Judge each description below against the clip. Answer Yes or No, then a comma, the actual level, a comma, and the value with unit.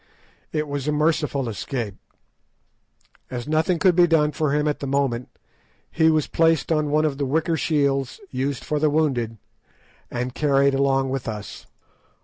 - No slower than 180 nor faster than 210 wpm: No, average, 160 wpm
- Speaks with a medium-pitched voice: Yes, medium, 145 Hz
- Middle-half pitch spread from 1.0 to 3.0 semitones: Yes, narrow, 2.5 semitones